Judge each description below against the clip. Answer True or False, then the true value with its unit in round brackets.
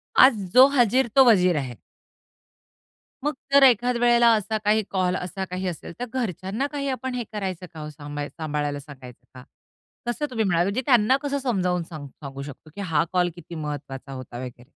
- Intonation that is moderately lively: False (8.2 semitones)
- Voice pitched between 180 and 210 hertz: True (185 Hz)